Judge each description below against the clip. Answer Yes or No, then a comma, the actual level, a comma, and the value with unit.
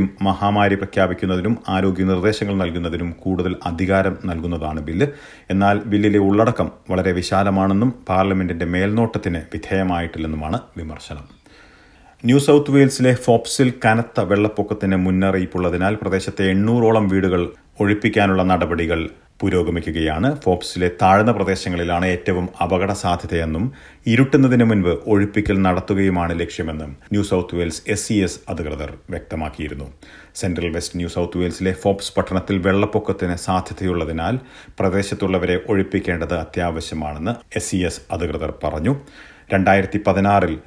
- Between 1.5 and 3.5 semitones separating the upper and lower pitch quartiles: Yes, average, 2.8 semitones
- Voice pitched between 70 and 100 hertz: Yes, very low, 95 Hz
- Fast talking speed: No, average, 95 wpm